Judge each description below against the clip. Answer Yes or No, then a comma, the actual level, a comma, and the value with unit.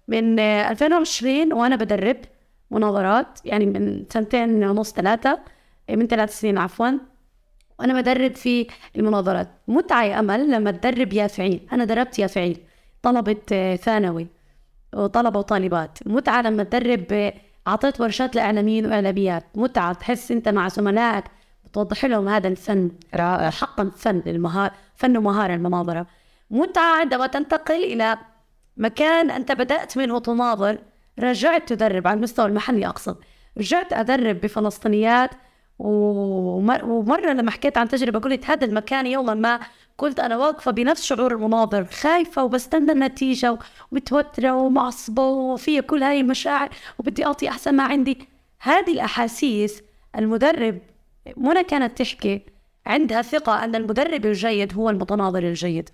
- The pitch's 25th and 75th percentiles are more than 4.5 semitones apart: No, average, 4.1 semitones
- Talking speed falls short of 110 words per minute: No, average, 125 wpm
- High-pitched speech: Yes, high, 230 Hz